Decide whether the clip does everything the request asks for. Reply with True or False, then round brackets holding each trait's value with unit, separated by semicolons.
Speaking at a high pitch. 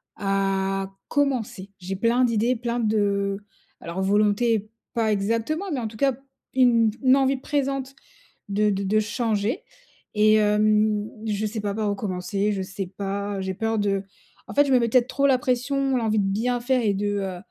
True (215 Hz)